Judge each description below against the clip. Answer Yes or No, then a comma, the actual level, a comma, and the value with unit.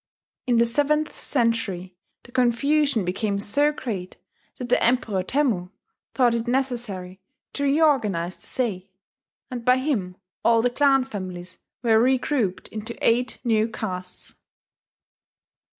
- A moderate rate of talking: No, slow, 125 wpm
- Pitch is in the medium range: No, high, 235 Hz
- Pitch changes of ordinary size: Yes, average, 4.9 semitones